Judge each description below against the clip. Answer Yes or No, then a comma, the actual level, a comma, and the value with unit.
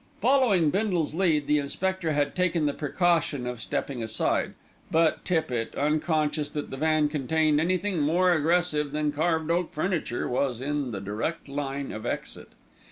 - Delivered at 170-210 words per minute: No, average, 155 wpm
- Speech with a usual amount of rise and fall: Yes, average, 3.2 semitones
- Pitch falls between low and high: Yes, medium, 155 Hz